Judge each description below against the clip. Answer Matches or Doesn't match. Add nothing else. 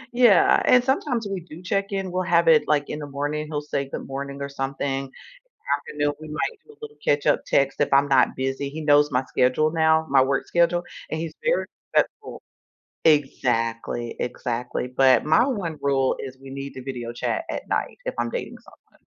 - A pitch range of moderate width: Matches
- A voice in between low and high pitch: Matches